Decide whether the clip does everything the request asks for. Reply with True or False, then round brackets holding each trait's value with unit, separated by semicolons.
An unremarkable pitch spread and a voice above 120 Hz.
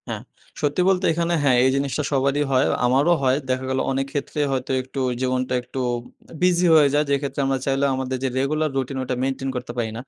False (1.8 semitones; 135 Hz)